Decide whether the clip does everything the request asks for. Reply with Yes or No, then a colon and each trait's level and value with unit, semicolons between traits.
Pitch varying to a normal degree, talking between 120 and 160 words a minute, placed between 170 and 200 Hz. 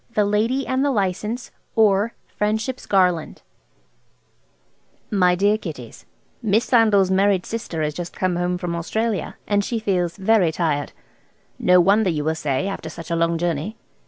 Yes: average, 4.2 semitones; average, 150 wpm; high, 190 Hz